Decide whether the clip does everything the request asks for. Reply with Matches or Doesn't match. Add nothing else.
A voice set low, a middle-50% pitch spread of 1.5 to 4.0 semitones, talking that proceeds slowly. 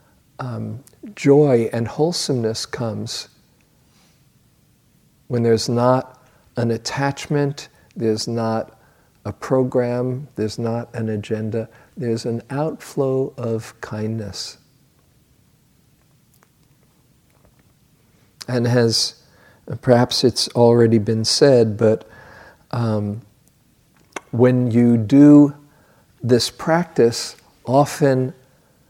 Matches